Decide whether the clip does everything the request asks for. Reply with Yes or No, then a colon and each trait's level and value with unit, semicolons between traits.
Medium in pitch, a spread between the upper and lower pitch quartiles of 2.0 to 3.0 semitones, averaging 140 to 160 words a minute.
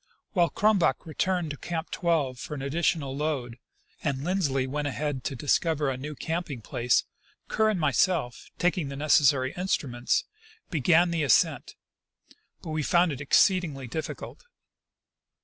No: medium, 150 Hz; average, 4.1 semitones; average, 145 wpm